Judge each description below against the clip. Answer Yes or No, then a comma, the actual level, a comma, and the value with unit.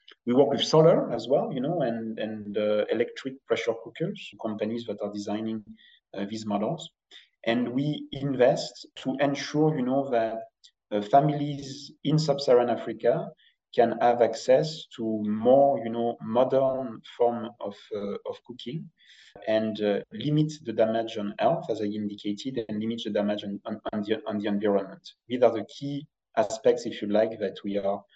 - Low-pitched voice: Yes, low, 115 Hz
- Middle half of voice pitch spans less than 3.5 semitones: No, average, 4.8 semitones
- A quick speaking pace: No, average, 165 wpm